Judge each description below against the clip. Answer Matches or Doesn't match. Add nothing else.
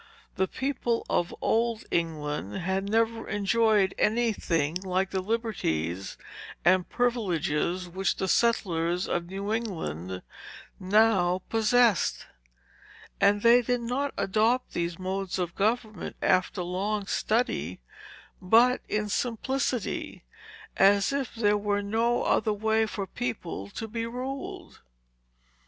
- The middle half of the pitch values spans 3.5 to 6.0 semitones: Matches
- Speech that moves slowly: Matches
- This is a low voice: Doesn't match